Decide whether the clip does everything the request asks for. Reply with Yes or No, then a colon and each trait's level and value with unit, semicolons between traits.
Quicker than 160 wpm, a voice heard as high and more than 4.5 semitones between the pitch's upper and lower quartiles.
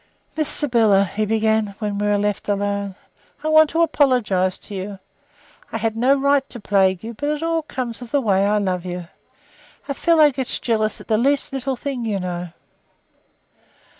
Yes: average, 185 wpm; high, 220 Hz; wide, 5.4 semitones